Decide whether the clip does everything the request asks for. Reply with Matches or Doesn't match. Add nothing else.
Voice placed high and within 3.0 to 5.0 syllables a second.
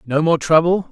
Doesn't match